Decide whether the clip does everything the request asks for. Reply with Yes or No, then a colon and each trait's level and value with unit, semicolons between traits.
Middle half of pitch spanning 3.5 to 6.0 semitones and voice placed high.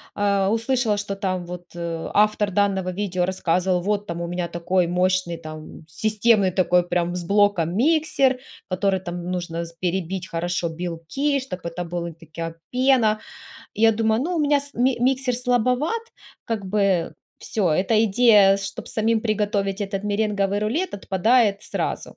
Yes: average, 3.9 semitones; high, 195 Hz